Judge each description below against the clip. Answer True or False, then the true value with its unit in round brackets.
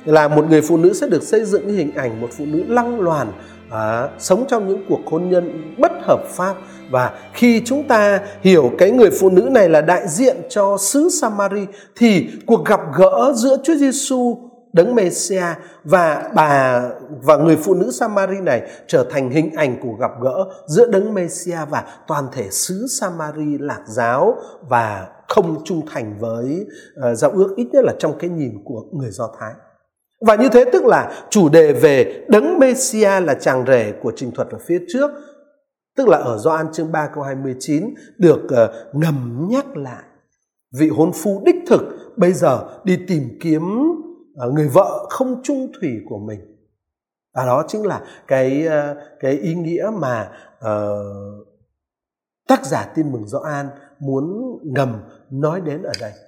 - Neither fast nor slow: True (175 wpm)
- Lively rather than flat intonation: True (8.5 semitones)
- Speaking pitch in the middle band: True (175 Hz)